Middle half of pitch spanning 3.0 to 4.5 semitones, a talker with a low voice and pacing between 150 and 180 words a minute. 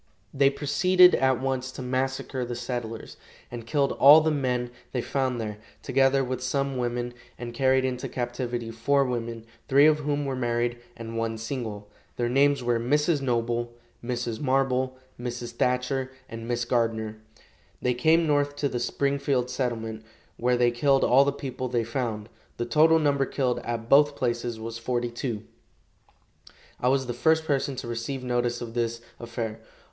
No: narrow, 2.5 semitones; low, 125 Hz; average, 165 wpm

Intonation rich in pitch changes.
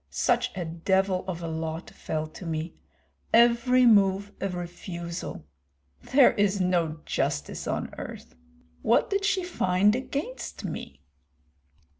Yes: wide, 5.9 semitones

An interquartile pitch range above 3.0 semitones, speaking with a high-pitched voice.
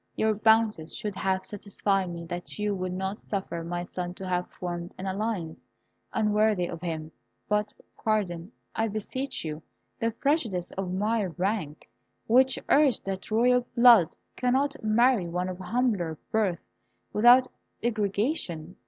Yes: average, 4.0 semitones; high, 200 Hz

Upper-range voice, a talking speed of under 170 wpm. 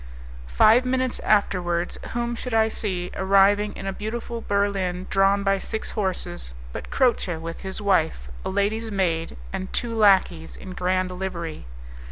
Yes: high, 195 Hz; average, 150 wpm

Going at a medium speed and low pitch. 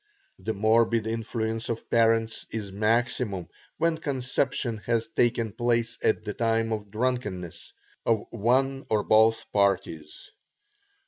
No: slow, 120 wpm; low, 115 Hz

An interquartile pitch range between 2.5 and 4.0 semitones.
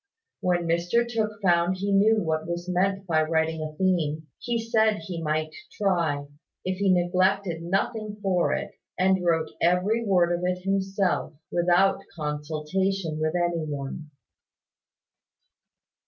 Yes: average, 3.2 semitones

